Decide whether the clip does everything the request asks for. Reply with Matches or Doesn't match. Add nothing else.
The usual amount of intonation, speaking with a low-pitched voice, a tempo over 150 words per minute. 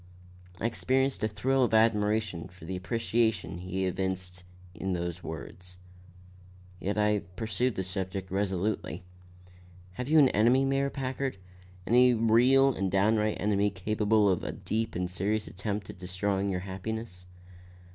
Doesn't match